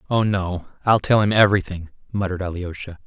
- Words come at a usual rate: Yes, average, 155 wpm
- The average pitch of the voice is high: No, very low, 95 Hz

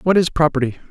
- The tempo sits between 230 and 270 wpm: No, average, 200 wpm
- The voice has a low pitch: No, medium, 155 Hz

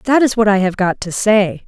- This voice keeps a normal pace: No, fast, 285 wpm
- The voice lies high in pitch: Yes, high, 210 Hz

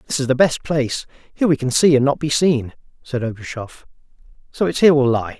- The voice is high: No, low, 135 Hz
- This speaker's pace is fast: Yes, fast, 220 wpm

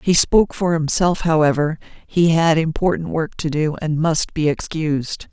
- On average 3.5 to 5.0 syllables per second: Yes, 4.7 syllables/s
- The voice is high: No, medium, 160 Hz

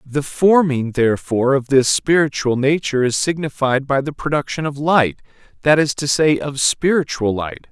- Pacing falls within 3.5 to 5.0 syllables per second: Yes, 4.9 syllables/s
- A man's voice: Yes, male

